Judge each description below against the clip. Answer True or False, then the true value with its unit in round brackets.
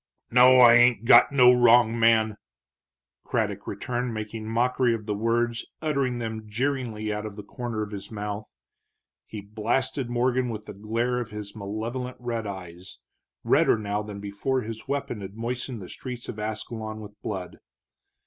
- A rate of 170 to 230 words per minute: False (160 wpm)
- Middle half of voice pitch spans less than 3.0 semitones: True (2.6 semitones)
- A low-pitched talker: True (115 Hz)